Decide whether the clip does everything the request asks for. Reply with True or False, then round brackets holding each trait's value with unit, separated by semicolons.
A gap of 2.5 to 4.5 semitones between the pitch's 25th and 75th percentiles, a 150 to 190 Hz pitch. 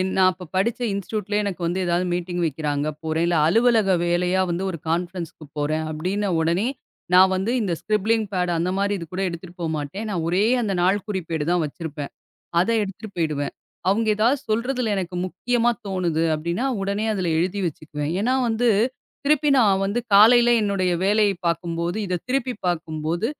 True (3.9 semitones; 185 Hz)